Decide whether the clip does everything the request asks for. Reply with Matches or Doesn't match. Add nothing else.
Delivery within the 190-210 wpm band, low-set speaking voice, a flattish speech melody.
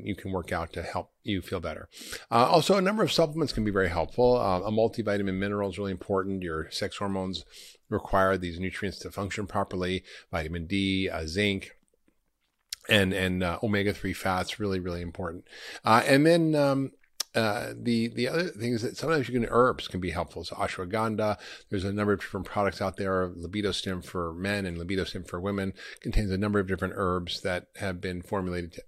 Doesn't match